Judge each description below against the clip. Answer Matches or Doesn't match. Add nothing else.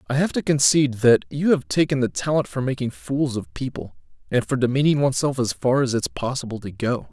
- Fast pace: Matches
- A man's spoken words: Matches